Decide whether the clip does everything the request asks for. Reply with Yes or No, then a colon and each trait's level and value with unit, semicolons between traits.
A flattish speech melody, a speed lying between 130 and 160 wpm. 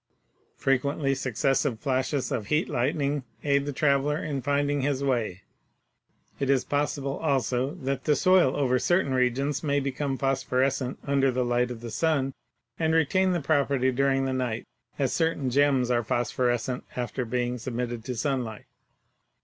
Yes: narrow, 2.3 semitones; average, 150 wpm